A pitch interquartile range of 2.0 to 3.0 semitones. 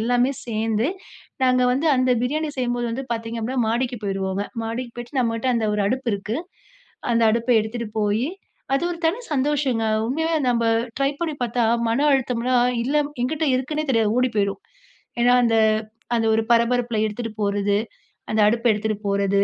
Yes: average, 2.7 semitones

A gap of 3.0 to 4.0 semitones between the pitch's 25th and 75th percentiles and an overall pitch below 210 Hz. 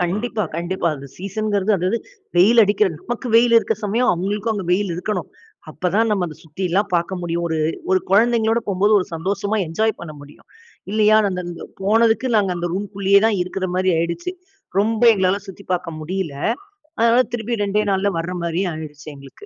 Yes: average, 3.7 semitones; high, 195 Hz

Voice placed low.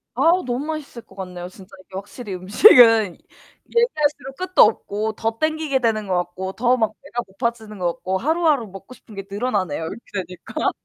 No: high, 225 Hz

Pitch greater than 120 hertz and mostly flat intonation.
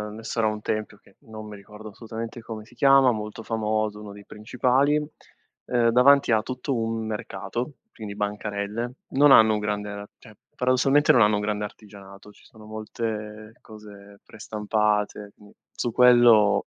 No: low, 110 Hz; narrow, 2.2 semitones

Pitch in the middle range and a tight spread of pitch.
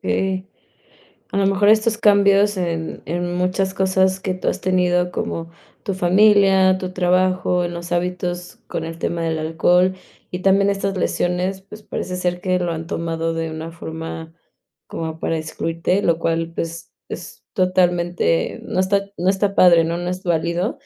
Yes: medium, 180 Hz; narrow, 2.2 semitones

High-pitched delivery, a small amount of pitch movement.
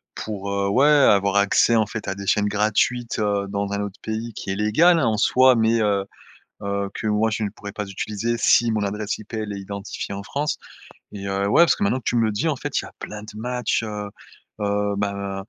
No: low, 105 Hz; narrow, 2.1 semitones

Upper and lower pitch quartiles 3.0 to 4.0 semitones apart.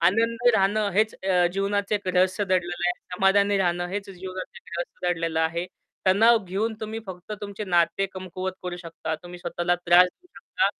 No: narrow, 2.5 semitones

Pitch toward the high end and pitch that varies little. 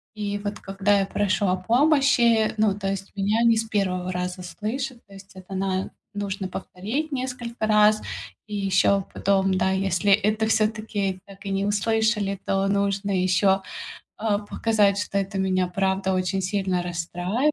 Yes: high, 200 Hz; narrow, 2.1 semitones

